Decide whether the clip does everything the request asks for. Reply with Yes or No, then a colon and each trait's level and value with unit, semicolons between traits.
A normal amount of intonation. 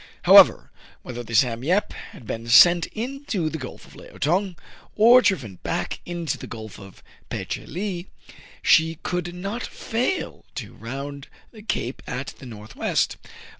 No: wide, 8.4 semitones